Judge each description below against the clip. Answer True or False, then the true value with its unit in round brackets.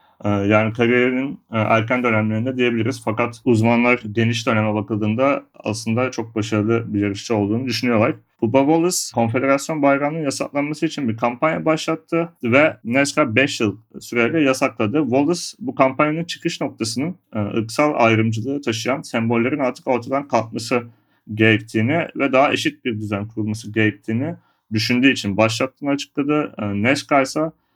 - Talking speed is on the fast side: False (125 wpm)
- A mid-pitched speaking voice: False (120 Hz)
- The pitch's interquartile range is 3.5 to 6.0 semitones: True (4.0 semitones)